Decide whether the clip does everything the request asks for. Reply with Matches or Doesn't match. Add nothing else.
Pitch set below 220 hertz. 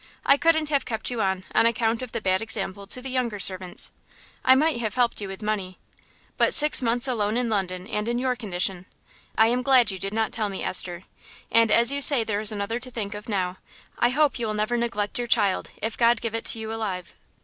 Doesn't match